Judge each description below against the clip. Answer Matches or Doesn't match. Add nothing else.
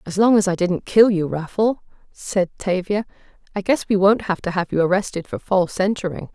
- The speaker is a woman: Matches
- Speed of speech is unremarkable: Doesn't match